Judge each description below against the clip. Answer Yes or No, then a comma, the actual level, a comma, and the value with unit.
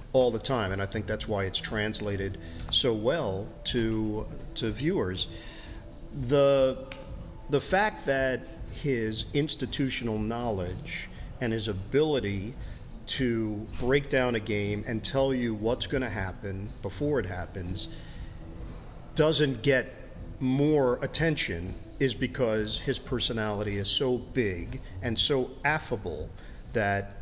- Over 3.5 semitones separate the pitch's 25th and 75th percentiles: Yes, average, 4.8 semitones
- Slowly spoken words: Yes, slow, 120 wpm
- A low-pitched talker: Yes, low, 115 Hz